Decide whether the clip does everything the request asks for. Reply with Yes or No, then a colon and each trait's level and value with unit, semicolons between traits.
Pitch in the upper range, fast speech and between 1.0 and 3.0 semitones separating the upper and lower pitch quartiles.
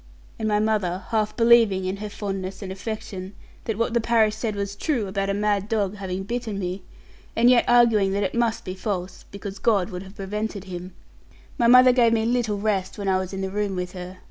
Yes: high, 205 Hz; fast, 220 wpm; average, 2.7 semitones